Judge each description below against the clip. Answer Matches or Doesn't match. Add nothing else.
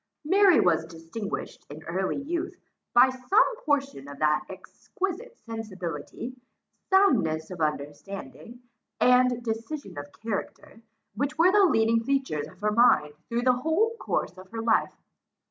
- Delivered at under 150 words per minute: Matches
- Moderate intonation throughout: Doesn't match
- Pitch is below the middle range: Doesn't match